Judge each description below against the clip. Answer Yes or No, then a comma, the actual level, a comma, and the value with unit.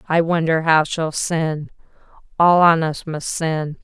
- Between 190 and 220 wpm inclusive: No, average, 155 wpm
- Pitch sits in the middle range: Yes, medium, 160 Hz